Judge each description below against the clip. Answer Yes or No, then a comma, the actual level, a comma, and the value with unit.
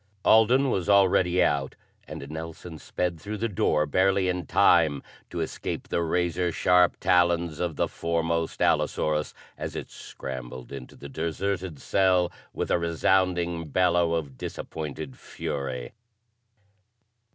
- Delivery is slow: Yes, slow, 130 wpm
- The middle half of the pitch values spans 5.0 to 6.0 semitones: No, average, 2.9 semitones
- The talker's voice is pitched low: Yes, very low, 85 Hz